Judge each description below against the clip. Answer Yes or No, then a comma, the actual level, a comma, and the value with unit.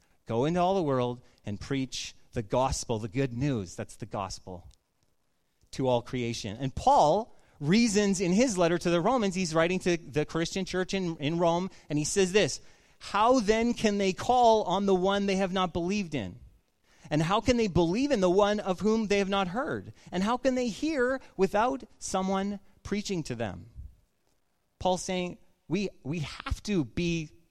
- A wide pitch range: Yes, wide, 7.0 semitones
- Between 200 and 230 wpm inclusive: No, average, 185 wpm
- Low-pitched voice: No, medium, 175 Hz